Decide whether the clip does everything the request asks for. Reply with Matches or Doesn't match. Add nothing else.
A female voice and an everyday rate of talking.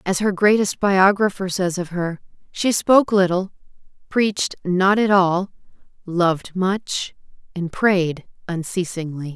Doesn't match